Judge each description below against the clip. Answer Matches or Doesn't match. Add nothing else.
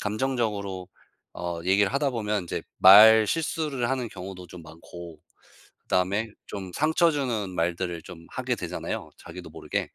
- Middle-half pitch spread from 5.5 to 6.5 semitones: Doesn't match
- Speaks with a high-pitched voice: Doesn't match